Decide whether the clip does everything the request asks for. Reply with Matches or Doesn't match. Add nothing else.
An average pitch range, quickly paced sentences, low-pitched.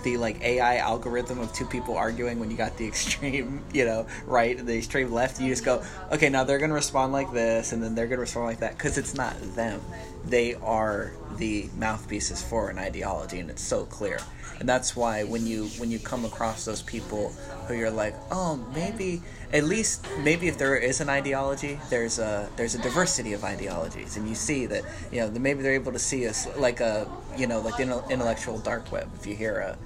Matches